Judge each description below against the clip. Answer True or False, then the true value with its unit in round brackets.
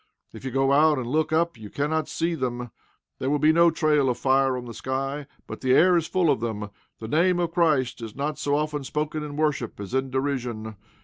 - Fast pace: True (230 wpm)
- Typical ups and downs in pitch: True (3.4 semitones)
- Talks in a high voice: False (140 Hz)